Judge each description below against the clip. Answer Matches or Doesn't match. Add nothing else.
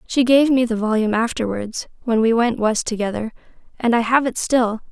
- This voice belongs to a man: Doesn't match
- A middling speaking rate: Matches